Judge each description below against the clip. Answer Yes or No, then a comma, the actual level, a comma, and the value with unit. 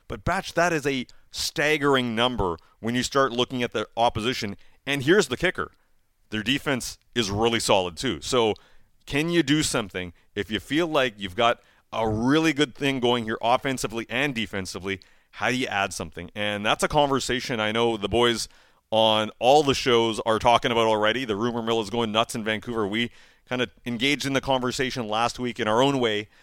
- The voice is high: No, low, 120 Hz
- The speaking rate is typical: Yes, average, 195 wpm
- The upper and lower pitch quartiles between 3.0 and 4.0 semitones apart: Yes, average, 3.5 semitones